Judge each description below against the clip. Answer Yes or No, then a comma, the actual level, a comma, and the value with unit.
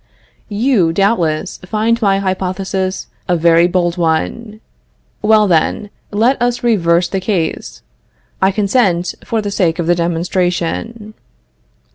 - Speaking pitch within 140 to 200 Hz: Yes, high, 190 Hz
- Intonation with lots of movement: No, average, 3.7 semitones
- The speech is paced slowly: Yes, slow, 120 wpm